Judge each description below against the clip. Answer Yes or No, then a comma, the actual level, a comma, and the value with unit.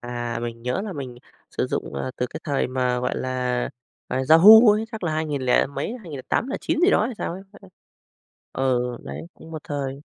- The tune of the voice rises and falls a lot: Yes, wide, 6.2 semitones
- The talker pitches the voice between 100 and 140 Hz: Yes, low, 135 Hz